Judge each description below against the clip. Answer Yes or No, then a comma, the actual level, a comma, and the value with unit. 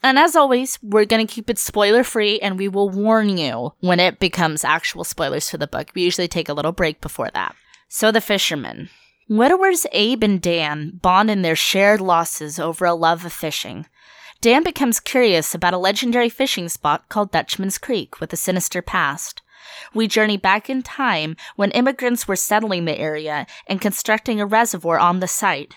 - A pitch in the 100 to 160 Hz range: No, high, 195 Hz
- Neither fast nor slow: Yes, average, 190 wpm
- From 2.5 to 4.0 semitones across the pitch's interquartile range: No, average, 4.9 semitones